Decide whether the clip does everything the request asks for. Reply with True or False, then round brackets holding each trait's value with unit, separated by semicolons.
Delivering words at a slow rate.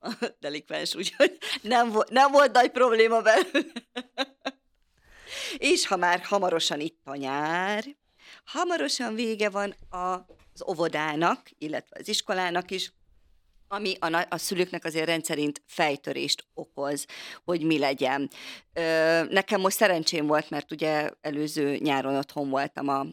False (115 wpm)